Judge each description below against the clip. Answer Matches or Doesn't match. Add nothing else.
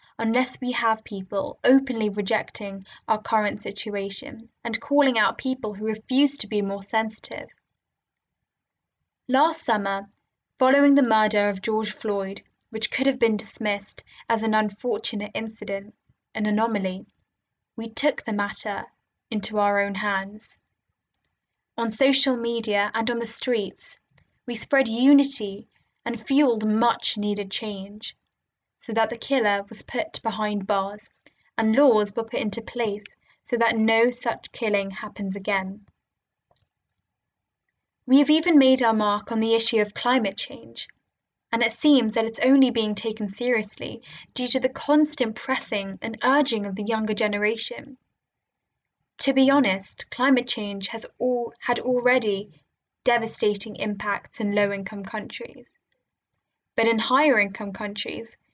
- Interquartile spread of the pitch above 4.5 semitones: Doesn't match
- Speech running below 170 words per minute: Matches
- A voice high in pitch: Matches